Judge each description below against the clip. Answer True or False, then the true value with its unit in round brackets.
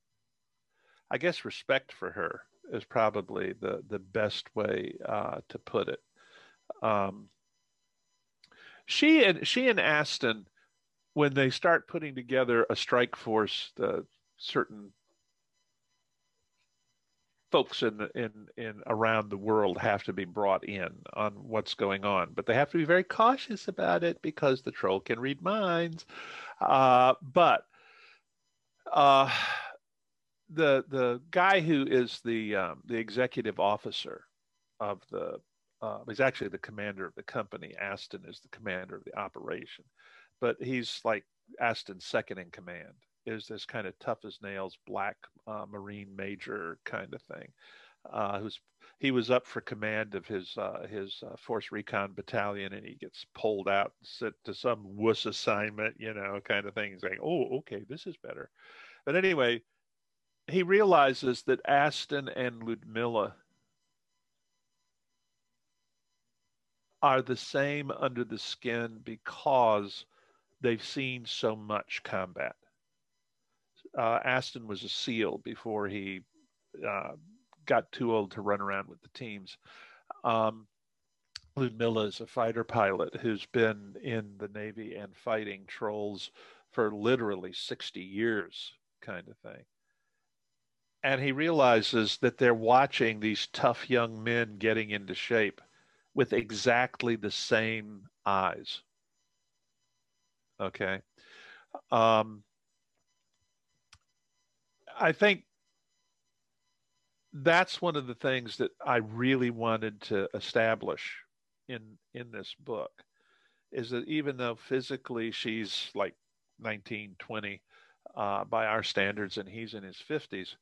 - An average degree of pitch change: True (3.8 semitones)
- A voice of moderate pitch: False (115 Hz)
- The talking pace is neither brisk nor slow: False (130 wpm)